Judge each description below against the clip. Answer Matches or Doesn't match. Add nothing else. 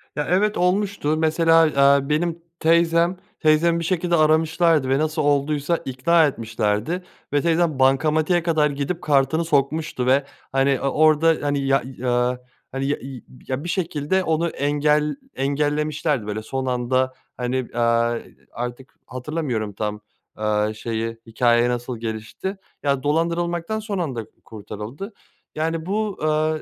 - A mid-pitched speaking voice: Matches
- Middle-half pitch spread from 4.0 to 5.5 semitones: Matches